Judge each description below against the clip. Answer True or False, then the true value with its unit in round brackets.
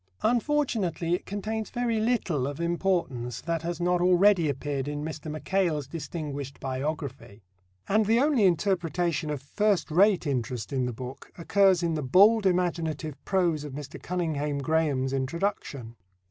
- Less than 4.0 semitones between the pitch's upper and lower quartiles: False (5.1 semitones)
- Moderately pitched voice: True (165 Hz)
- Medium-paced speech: True (145 wpm)